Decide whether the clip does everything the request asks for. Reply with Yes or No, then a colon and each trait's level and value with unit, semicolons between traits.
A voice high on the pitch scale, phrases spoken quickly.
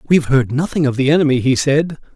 No: medium, 140 Hz; fast, 250 wpm